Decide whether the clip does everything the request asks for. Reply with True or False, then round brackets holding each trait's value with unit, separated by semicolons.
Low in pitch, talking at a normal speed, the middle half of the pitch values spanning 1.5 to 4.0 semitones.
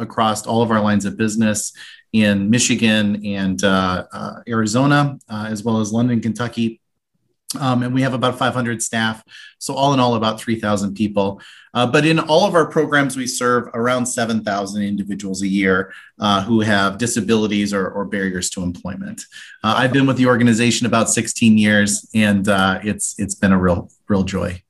True (110 Hz; 180 wpm; 3.3 semitones)